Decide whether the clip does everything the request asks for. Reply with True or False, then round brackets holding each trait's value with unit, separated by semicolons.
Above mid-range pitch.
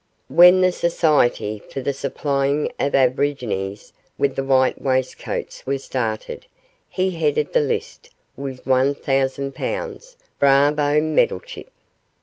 False (140 Hz)